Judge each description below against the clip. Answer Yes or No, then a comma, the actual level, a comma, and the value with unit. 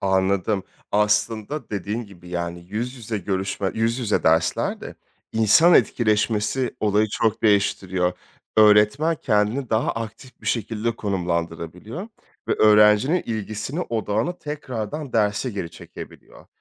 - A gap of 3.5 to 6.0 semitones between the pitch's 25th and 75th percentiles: No, average, 2.8 semitones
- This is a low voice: Yes, low, 105 Hz